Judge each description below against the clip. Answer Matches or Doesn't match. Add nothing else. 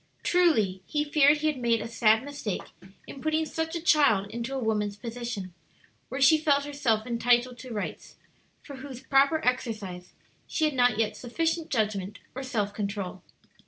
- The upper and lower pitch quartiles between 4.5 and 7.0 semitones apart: Matches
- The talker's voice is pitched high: Matches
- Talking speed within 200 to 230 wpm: Doesn't match